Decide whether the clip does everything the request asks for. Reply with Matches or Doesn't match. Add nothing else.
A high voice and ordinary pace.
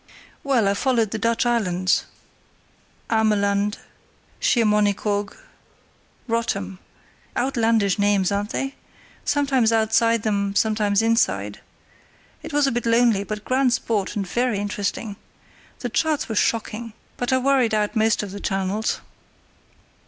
Doesn't match